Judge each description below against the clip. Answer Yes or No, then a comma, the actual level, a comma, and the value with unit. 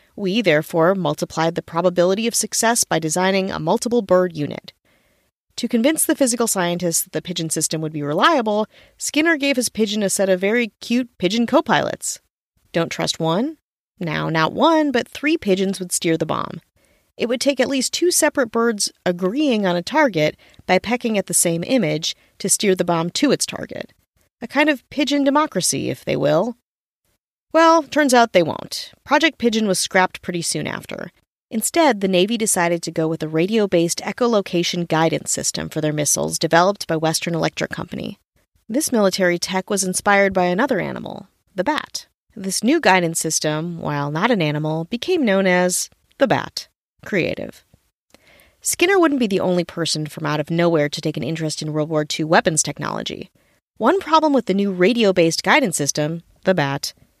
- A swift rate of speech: No, average, 180 wpm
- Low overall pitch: No, medium, 185 Hz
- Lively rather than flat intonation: Yes, wide, 6.5 semitones